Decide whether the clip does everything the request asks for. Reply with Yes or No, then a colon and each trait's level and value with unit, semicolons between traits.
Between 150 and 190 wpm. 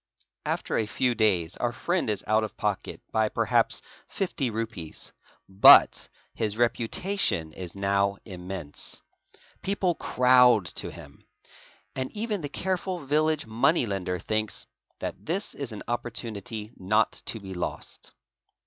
No: slow, 135 wpm